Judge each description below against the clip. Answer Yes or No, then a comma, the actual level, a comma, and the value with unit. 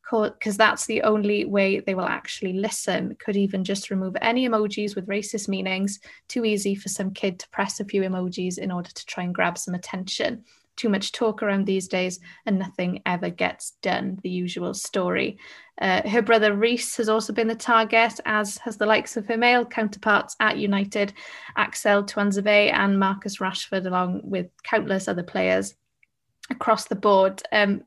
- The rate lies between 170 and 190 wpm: Yes, average, 180 wpm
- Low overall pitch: No, high, 205 Hz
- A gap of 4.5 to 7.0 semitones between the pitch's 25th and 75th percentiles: No, narrow, 2.6 semitones